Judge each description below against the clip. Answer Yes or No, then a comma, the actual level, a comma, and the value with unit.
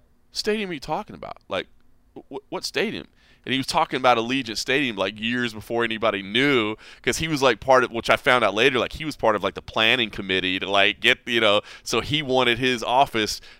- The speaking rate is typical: No, fast, 225 wpm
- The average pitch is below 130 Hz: Yes, low, 120 Hz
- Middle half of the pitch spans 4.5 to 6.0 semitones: No, average, 3.5 semitones